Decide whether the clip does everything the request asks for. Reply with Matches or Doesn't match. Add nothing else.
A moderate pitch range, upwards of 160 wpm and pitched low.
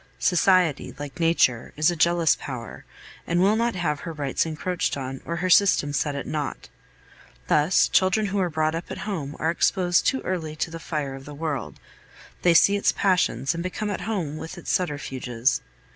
Doesn't match